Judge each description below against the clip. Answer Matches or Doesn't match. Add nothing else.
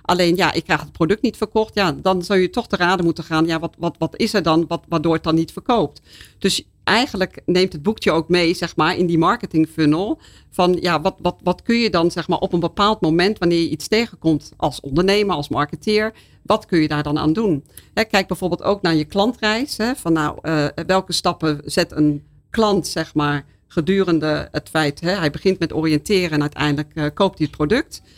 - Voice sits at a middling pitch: Matches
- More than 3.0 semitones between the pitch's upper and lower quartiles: Matches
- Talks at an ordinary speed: Doesn't match